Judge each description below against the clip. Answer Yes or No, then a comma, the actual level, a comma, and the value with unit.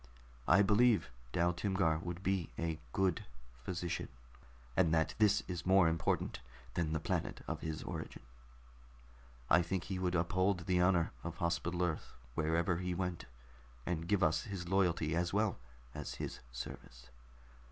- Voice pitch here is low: Yes, very low, 85 Hz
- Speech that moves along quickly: No, average, 150 wpm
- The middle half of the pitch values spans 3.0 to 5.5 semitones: No, narrow, 2.4 semitones